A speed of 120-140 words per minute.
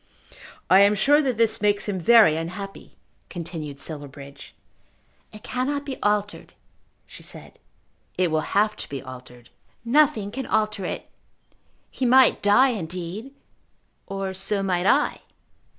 Yes: slow, 135 wpm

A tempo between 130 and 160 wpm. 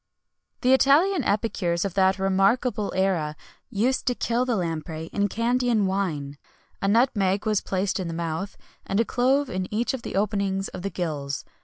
No: average, 170 wpm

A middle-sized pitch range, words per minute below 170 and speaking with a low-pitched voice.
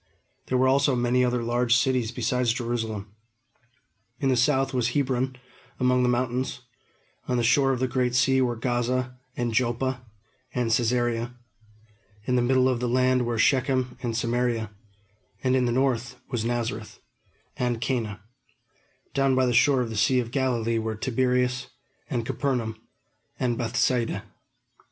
No: narrow, 1.5 semitones; average, 150 wpm; low, 125 Hz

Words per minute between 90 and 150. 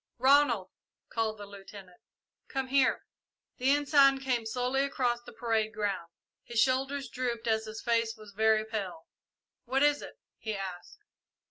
Yes: average, 145 wpm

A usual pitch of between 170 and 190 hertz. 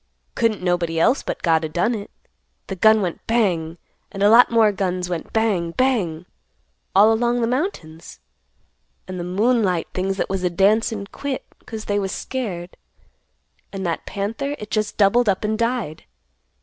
No: high, 200 Hz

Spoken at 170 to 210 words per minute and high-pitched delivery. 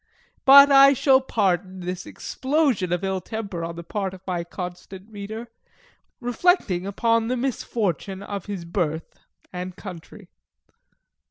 No: slow, 135 wpm; high, 195 Hz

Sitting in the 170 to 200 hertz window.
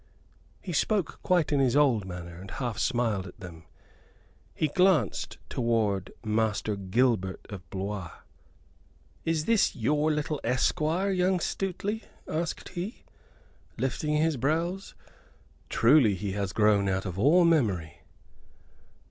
No: low, 125 Hz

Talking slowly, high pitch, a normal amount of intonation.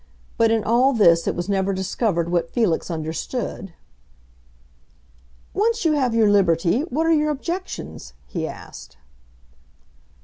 No: slow, 130 wpm; high, 215 Hz; wide, 7.9 semitones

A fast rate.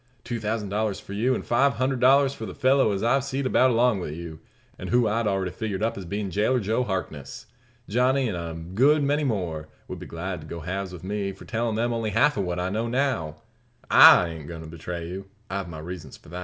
Yes: fast, 235 wpm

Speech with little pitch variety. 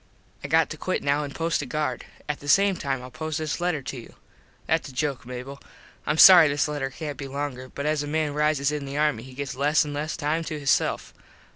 Yes: narrow, 1.9 semitones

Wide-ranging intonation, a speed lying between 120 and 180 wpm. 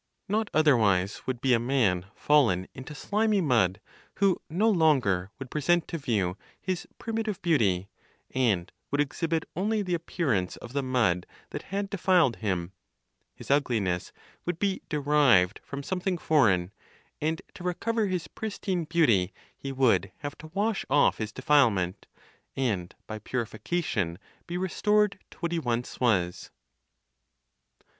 Yes: wide, 8.7 semitones; average, 140 wpm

